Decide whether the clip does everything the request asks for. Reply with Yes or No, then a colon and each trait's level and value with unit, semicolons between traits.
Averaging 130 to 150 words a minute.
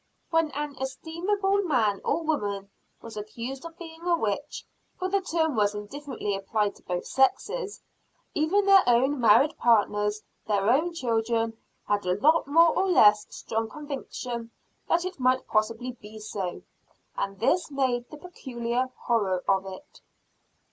Yes: average, 145 wpm